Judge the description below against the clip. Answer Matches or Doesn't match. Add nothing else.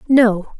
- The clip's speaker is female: Matches